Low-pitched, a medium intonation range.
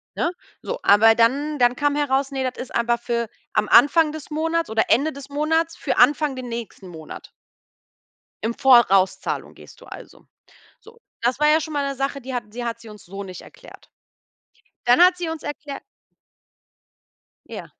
No: very high, 265 Hz; average, 4.4 semitones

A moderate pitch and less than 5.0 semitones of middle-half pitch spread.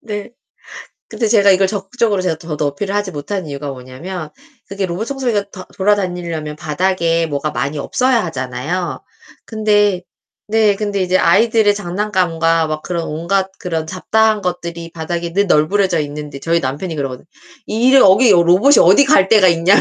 Yes: medium, 180 Hz; average, 4.2 semitones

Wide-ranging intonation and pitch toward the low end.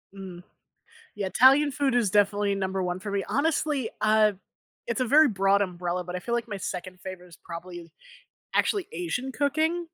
No: wide, 6.2 semitones; high, 205 Hz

